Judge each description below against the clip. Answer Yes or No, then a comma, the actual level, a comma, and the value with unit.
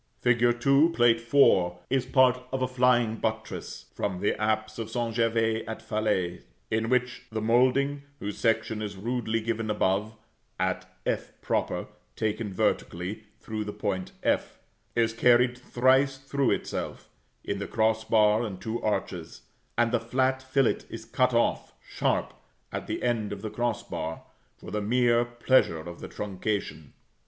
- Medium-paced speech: Yes, average, 155 wpm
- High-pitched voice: No, low, 115 Hz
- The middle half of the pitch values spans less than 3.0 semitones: Yes, narrow, 2.5 semitones